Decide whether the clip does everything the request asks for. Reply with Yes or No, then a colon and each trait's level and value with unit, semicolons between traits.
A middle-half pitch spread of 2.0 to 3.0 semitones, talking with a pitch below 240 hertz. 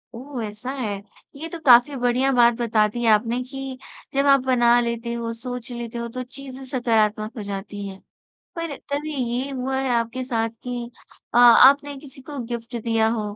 No: narrow, 2.5 semitones; high, 245 Hz